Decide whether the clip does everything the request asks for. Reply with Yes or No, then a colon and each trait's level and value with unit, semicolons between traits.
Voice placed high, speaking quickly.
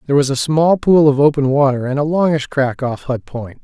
No: medium, 140 Hz; fast, 250 wpm